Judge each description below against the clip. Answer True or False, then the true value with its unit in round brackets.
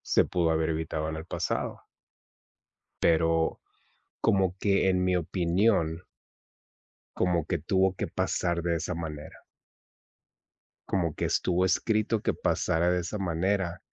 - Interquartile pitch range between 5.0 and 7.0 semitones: False (2.4 semitones)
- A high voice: False (85 Hz)